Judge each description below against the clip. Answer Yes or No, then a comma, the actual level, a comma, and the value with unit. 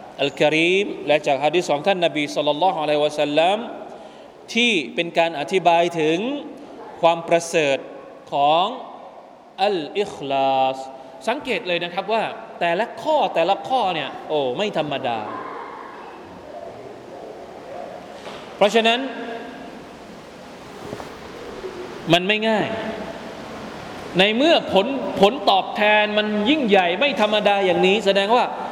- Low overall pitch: No, high, 200 Hz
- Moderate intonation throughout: No, wide, 5.7 semitones